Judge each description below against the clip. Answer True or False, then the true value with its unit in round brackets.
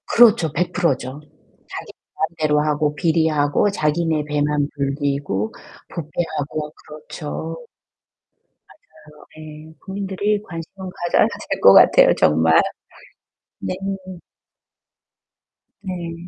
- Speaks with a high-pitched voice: False (155 Hz)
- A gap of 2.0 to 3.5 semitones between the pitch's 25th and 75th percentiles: True (2.7 semitones)